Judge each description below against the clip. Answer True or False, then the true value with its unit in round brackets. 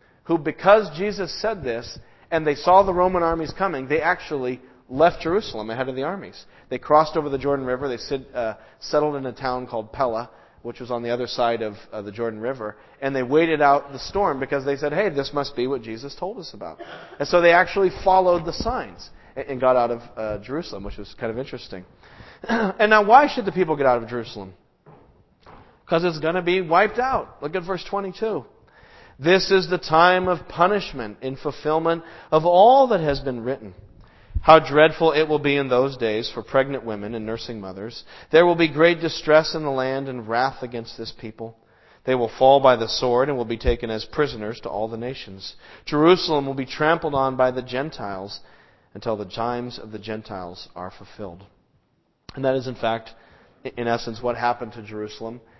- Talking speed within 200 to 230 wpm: True (205 wpm)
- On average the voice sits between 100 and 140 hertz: True (135 Hz)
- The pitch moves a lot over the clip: True (6.2 semitones)